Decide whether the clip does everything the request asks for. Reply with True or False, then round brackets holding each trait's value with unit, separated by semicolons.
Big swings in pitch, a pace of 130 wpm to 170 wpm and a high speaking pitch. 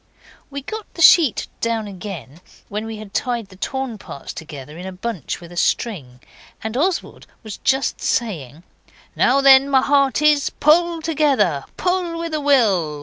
True (7.6 semitones; 155 wpm; 235 Hz)